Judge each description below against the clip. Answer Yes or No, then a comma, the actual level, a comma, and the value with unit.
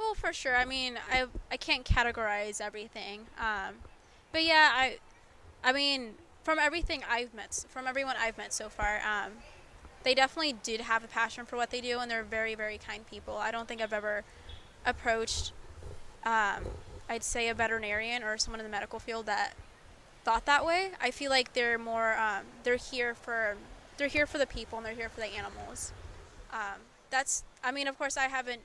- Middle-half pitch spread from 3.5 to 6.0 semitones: No, average, 3.0 semitones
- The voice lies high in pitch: Yes, high, 235 Hz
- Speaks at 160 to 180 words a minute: No, average, 195 wpm